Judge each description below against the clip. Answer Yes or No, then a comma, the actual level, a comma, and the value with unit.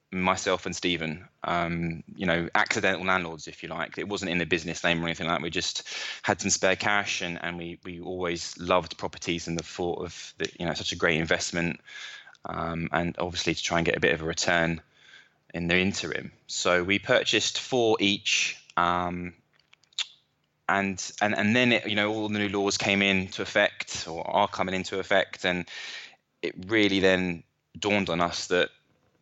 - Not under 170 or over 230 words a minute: Yes, average, 190 wpm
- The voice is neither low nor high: No, very low, 90 Hz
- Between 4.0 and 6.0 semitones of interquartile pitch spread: No, narrow, 2.4 semitones